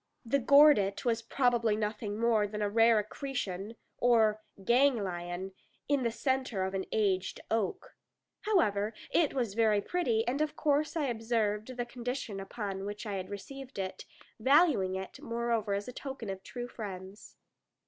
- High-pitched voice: Yes, high, 225 Hz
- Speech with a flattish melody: No, average, 3.8 semitones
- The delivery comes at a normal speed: Yes, average, 155 wpm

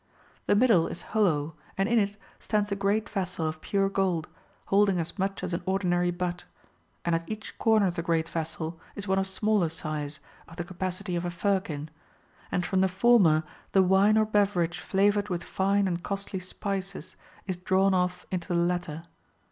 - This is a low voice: No, medium, 185 Hz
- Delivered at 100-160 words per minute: No, average, 185 wpm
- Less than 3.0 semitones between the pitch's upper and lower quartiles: Yes, narrow, 2.6 semitones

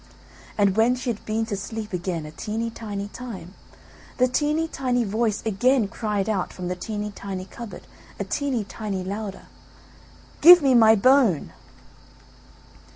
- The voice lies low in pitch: No, high, 215 Hz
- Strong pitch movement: No, average, 3.7 semitones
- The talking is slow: No, average, 150 wpm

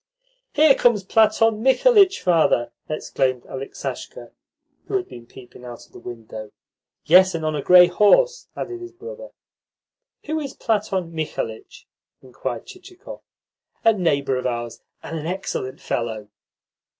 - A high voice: No, medium, 180 Hz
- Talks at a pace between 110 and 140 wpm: Yes, slow, 135 wpm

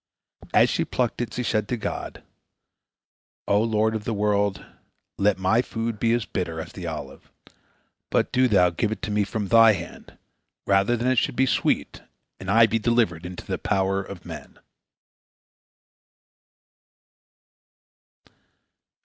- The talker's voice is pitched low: Yes, low, 105 Hz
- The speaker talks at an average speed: Yes, average, 150 wpm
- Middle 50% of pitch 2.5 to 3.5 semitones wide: Yes, average, 3.0 semitones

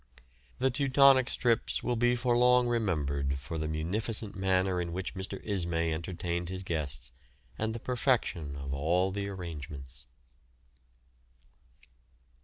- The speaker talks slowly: Yes, slow, 125 wpm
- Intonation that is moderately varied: No, wide, 6.7 semitones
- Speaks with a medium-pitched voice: No, very low, 95 Hz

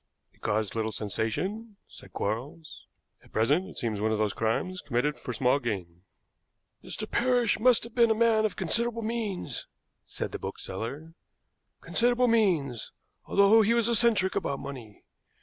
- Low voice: No, medium, 165 Hz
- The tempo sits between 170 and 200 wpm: No, average, 150 wpm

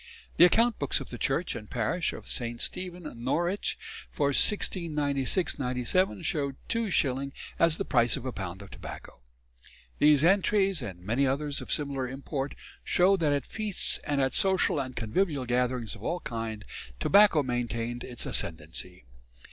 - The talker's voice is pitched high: No, medium, 140 Hz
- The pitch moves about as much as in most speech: No, wide, 6.2 semitones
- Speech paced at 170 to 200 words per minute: No, average, 155 wpm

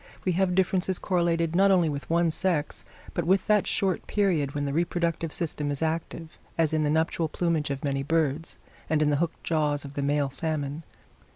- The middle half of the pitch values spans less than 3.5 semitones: Yes, average, 2.8 semitones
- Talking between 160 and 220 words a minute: Yes, average, 195 wpm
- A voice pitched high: No, medium, 160 Hz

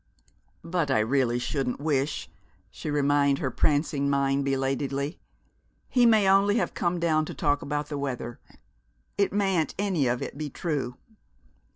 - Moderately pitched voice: Yes, medium, 145 Hz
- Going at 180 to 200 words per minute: No, average, 150 wpm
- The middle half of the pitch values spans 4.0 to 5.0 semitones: No, average, 3.6 semitones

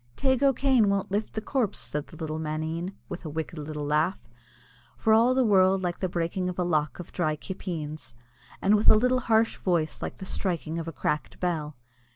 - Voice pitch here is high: No, medium, 180 Hz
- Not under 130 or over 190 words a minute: No, average, 200 wpm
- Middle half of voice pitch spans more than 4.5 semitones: Yes, average, 5.2 semitones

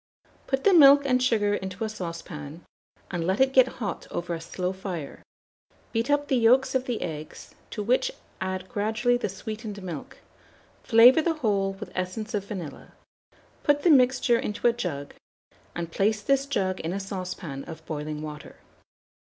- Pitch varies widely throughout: Yes, wide, 5.9 semitones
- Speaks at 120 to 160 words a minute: No, average, 170 wpm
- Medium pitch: No, high, 205 Hz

